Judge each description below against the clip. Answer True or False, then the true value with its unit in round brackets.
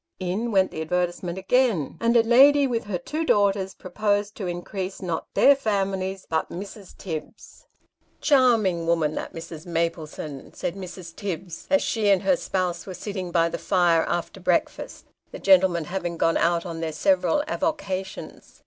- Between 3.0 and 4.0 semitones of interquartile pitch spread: True (3.5 semitones)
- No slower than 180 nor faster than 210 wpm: False (165 wpm)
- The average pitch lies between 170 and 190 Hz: True (185 Hz)